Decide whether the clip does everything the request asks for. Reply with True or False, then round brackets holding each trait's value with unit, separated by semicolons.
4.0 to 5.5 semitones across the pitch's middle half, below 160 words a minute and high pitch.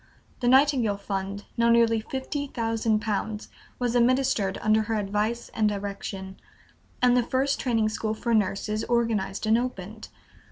False (2.6 semitones; 145 wpm; 220 Hz)